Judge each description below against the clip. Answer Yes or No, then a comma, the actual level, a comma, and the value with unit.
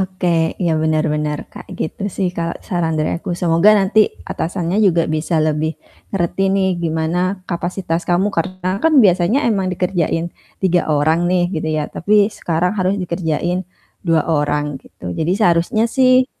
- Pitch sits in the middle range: Yes, medium, 175 Hz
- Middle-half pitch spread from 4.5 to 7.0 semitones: No, average, 2.9 semitones